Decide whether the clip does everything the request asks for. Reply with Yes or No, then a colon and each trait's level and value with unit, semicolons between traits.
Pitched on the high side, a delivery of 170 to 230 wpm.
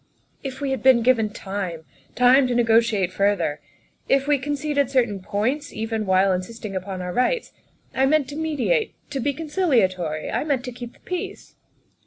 Yes: high, 245 Hz; average, 175 wpm